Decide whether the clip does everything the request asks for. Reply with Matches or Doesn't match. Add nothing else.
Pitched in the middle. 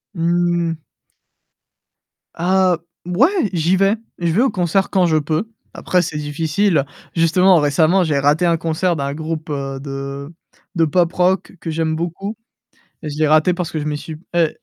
Matches